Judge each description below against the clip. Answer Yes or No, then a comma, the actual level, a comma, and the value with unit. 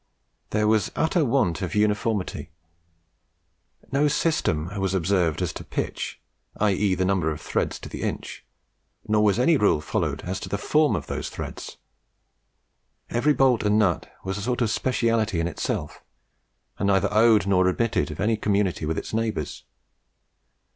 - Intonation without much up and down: No, average, 3.7 semitones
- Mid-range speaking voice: No, low, 105 Hz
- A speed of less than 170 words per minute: Yes, average, 160 wpm